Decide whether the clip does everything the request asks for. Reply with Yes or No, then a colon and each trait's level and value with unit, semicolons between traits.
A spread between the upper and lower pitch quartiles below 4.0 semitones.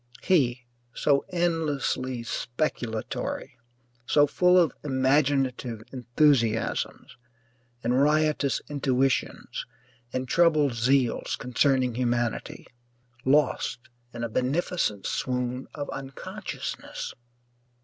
Yes: average, 3.4 semitones